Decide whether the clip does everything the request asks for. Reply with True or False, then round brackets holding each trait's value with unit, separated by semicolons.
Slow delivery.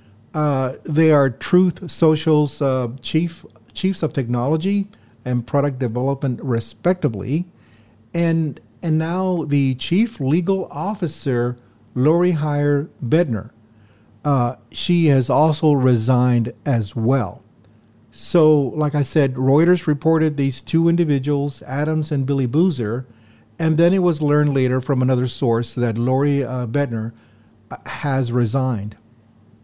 True (120 wpm)